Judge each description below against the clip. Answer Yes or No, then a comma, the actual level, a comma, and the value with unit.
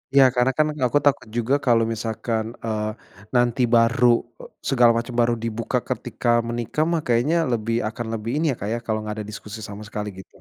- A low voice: Yes, low, 115 Hz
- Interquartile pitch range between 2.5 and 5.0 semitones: No, narrow, 2.1 semitones